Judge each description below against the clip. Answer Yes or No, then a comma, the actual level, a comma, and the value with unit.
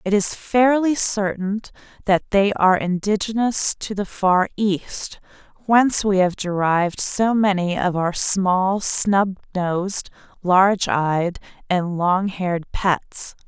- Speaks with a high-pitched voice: Yes, high, 195 Hz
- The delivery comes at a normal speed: No, slow, 130 wpm